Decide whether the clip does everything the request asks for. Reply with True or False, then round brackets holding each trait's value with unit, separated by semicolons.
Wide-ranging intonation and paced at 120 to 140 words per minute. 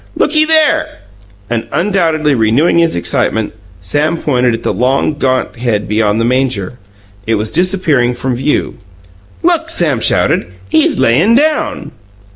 True (6.8 semitones; 135 wpm)